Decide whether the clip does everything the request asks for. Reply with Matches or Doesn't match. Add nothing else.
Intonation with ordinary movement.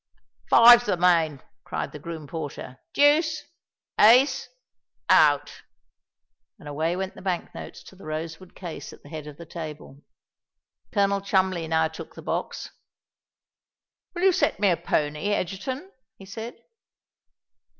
Matches